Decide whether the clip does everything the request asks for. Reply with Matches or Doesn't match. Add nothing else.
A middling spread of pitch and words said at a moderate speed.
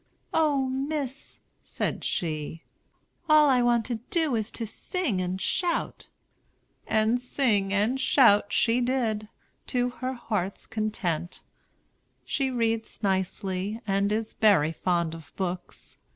Doesn't match